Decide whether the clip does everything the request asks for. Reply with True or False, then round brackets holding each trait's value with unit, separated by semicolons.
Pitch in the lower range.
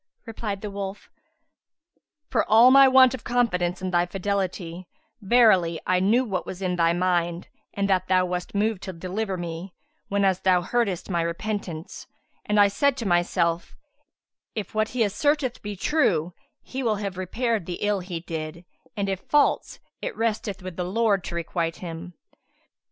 False (190 Hz)